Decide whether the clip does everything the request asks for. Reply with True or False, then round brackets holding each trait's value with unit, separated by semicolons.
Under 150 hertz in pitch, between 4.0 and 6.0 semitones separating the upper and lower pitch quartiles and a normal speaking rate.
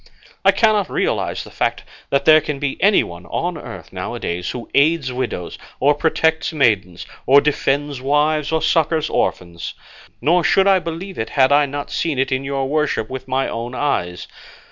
False (140 Hz; 3.6 semitones; 180 wpm)